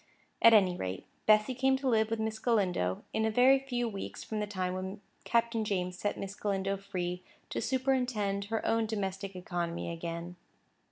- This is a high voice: Yes, high, 205 Hz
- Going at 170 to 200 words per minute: Yes, average, 175 wpm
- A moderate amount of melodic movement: Yes, average, 3.6 semitones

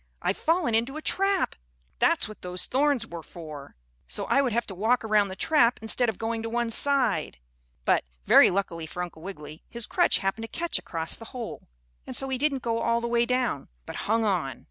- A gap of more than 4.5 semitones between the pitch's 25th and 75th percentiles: Yes, average, 5.3 semitones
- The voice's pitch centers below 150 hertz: No, high, 225 Hz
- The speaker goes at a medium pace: No, fast, 210 wpm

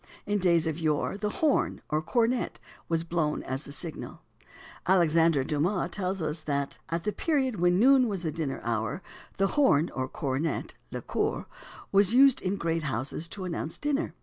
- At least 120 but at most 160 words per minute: No, average, 175 wpm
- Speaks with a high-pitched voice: No, medium, 170 Hz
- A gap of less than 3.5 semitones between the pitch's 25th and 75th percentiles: No, average, 5.0 semitones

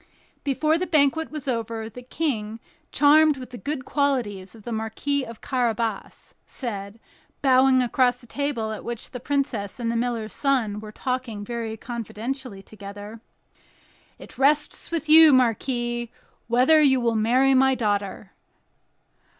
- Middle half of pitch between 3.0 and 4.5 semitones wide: Yes, average, 3.6 semitones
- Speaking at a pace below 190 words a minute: Yes, average, 140 wpm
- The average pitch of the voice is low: No, high, 245 Hz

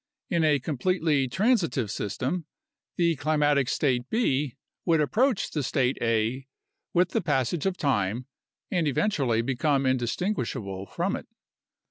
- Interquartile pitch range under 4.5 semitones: No, average, 5.3 semitones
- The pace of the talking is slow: Yes, slow, 125 wpm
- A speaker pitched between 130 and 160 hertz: Yes, medium, 140 Hz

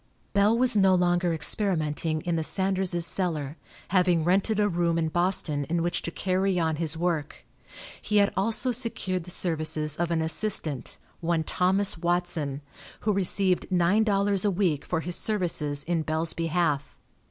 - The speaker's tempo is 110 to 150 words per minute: No, average, 160 wpm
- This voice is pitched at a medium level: Yes, medium, 175 Hz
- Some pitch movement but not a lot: Yes, average, 3.1 semitones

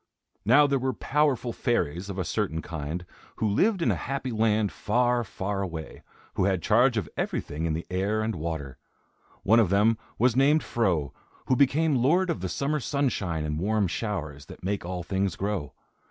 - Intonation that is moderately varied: No, wide, 6.3 semitones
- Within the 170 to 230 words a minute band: Yes, average, 185 wpm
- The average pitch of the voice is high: No, low, 105 Hz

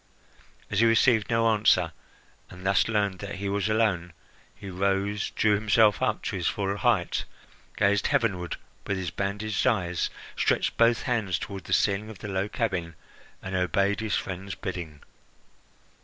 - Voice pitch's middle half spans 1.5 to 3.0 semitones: Yes, narrow, 2.4 semitones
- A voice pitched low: Yes, low, 100 Hz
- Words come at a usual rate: Yes, average, 155 wpm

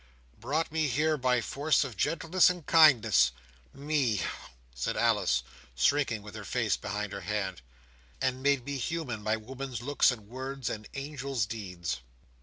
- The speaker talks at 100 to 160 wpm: Yes, average, 150 wpm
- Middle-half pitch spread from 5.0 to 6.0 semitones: Yes, wide, 5.4 semitones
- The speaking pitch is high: No, low, 130 Hz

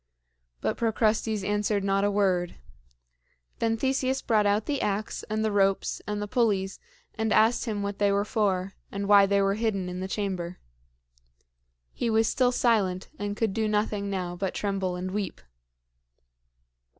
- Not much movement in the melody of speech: Yes, narrow, 2.0 semitones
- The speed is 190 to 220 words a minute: No, average, 160 wpm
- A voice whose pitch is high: Yes, high, 205 Hz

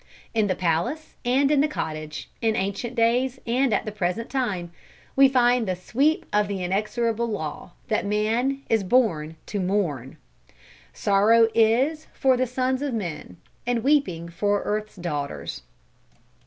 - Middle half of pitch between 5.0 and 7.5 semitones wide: Yes, average, 5.3 semitones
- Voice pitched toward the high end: Yes, high, 220 Hz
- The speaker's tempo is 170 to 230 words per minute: No, average, 150 wpm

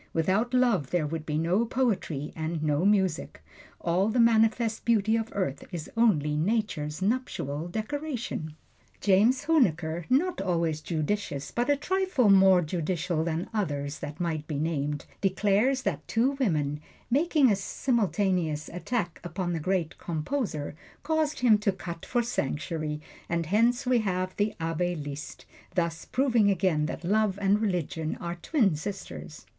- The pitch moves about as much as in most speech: No, wide, 6.1 semitones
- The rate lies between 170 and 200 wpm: No, average, 145 wpm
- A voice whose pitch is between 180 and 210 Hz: Yes, medium, 185 Hz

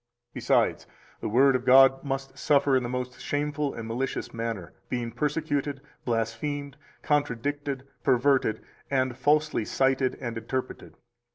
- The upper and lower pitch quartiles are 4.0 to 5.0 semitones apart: No, average, 2.8 semitones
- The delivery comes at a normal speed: No, slow, 125 wpm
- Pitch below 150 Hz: Yes, low, 135 Hz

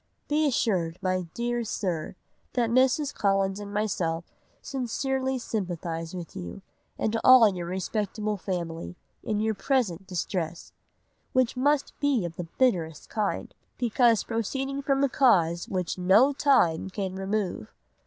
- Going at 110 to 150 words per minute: Yes, slow, 135 wpm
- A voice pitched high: Yes, high, 210 Hz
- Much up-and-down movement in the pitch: Yes, wide, 6.0 semitones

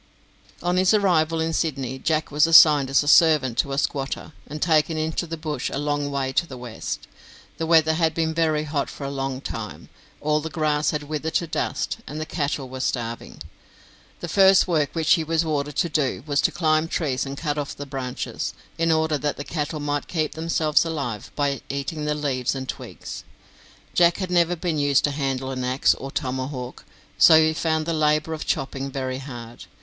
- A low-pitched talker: No, medium, 150 Hz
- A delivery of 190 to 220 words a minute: Yes, average, 200 wpm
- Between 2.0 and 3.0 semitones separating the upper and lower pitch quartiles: Yes, average, 2.7 semitones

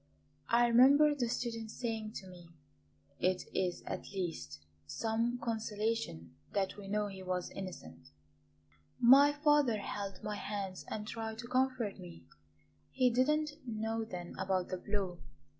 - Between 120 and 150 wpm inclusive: Yes, average, 140 wpm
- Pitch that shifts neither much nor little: Yes, average, 4.2 semitones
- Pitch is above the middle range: Yes, high, 215 Hz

